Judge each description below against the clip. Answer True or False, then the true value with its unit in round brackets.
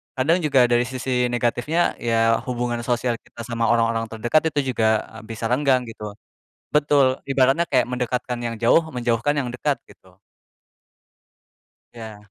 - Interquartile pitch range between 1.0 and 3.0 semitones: True (2.5 semitones)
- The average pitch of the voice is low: True (120 Hz)